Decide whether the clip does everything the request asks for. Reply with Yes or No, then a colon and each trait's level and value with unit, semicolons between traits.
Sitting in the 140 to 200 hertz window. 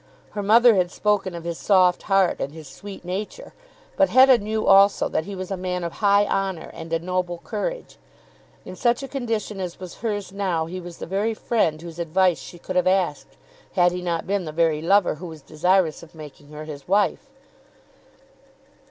Yes: medium, 185 Hz